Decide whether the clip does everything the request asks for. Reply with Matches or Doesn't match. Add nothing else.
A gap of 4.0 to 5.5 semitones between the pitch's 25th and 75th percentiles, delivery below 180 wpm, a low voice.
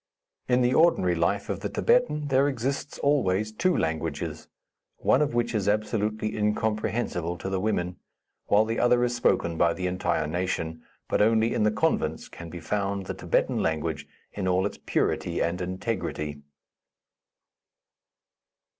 Matches